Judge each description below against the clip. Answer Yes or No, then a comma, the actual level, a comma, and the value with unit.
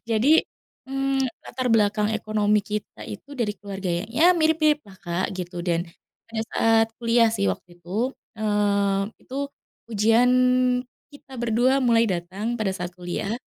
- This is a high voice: Yes, high, 215 Hz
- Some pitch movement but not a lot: Yes, average, 3.4 semitones